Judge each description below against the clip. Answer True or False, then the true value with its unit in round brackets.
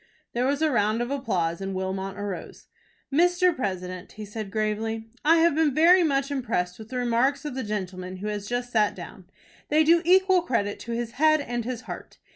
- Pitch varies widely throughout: True (6.1 semitones)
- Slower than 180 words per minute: False (200 wpm)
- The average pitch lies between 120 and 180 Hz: False (235 Hz)